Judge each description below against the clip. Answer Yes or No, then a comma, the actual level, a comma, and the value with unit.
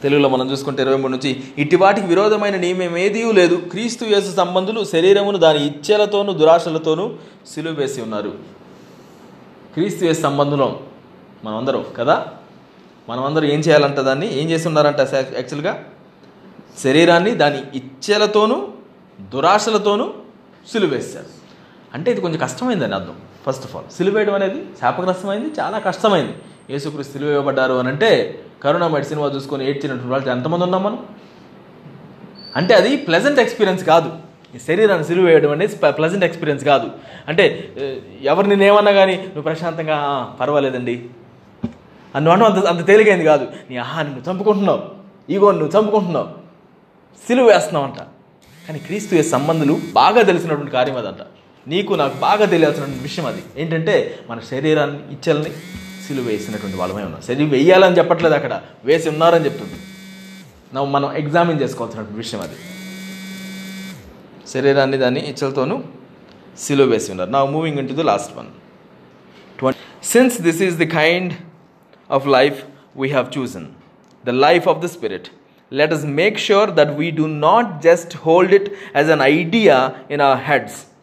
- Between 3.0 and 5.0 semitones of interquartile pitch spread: No, wide, 5.4 semitones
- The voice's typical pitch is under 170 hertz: Yes, medium, 160 Hz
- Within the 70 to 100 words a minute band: No, average, 115 wpm